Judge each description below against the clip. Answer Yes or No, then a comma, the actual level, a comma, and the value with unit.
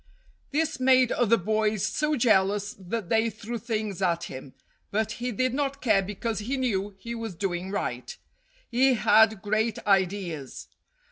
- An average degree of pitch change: Yes, average, 3.6 semitones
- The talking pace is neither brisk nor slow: Yes, average, 150 wpm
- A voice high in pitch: Yes, high, 220 Hz